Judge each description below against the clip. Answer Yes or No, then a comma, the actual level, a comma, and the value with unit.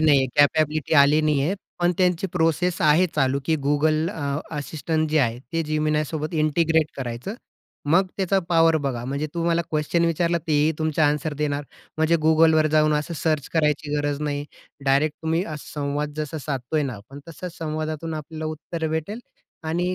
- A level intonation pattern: Yes, narrow, 2.0 semitones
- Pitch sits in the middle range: Yes, medium, 155 Hz